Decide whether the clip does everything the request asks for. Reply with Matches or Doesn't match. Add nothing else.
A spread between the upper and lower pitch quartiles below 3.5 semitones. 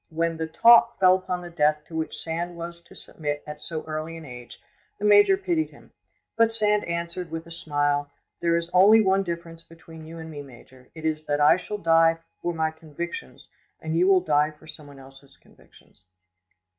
Matches